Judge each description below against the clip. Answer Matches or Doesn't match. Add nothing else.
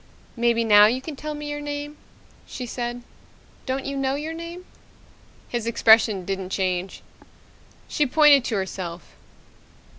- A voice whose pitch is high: Matches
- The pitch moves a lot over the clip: Matches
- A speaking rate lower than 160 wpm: Matches